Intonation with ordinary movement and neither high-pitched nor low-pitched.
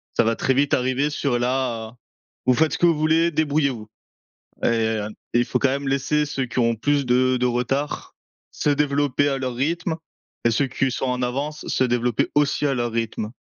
No: average, 3.1 semitones; low, 130 Hz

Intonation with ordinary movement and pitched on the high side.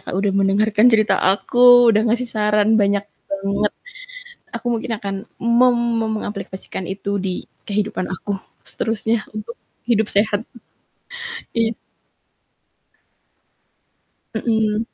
No: narrow, 2.3 semitones; high, 210 Hz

